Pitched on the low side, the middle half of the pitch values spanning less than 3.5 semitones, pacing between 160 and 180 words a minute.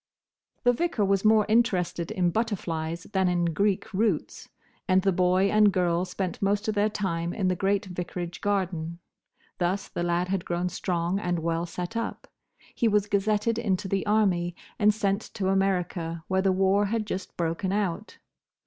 No: high, 190 Hz; average, 2.8 semitones; average, 170 wpm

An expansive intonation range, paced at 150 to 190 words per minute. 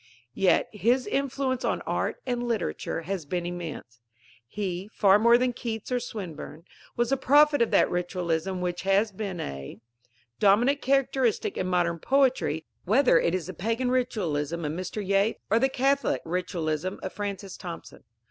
Yes: wide, 5.7 semitones; average, 155 wpm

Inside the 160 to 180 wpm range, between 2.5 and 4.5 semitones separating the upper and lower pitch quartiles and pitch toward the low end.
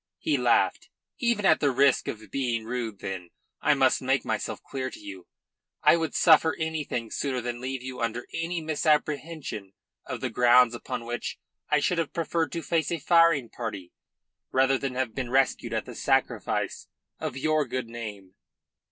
No: average, 170 wpm; average, 5.0 semitones; low, 130 Hz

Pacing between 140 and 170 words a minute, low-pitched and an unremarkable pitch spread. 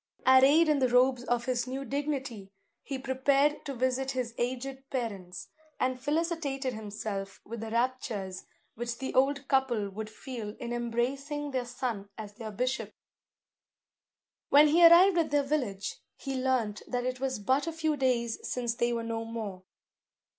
No: average, 160 wpm; very high, 255 Hz; average, 3.0 semitones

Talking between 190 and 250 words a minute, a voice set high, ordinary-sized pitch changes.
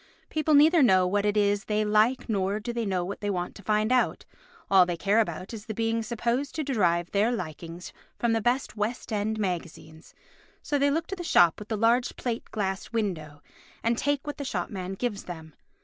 Yes: average, 200 wpm; high, 210 Hz; average, 4.3 semitones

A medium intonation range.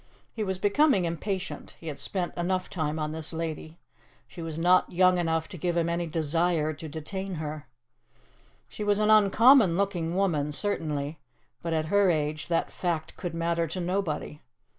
Yes: average, 3.2 semitones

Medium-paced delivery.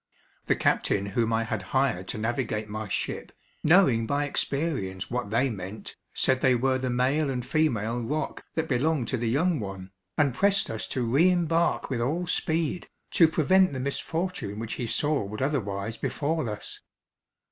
Yes: average, 170 wpm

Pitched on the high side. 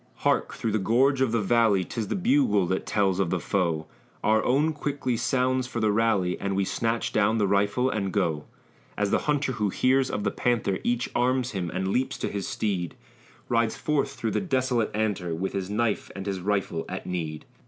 No: low, 110 Hz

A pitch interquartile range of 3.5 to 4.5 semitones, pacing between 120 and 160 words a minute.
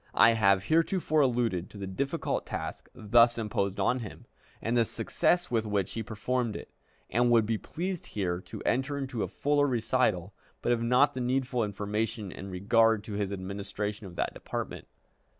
No: average, 3.8 semitones; average, 175 wpm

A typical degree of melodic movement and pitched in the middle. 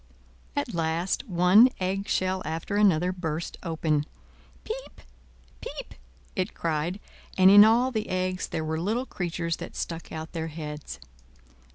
Yes: average, 3.3 semitones; medium, 180 Hz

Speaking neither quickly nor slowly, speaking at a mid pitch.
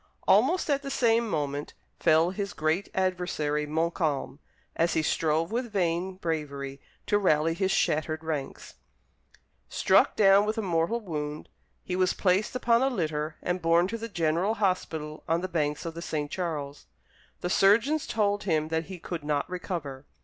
Yes: average, 165 wpm; medium, 170 Hz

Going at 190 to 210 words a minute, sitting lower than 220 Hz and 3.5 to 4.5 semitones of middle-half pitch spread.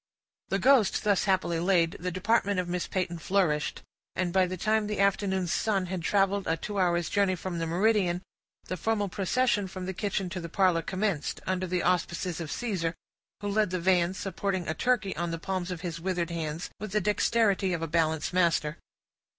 No: average, 195 wpm; medium, 185 Hz; narrow, 2.6 semitones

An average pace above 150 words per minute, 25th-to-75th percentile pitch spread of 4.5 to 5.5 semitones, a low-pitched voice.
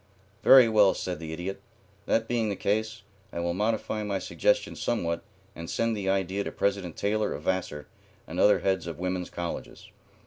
No: average, 175 wpm; average, 3.7 semitones; very low, 95 Hz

